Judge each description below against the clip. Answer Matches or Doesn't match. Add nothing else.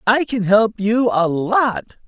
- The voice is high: Matches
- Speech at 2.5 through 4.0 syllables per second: Matches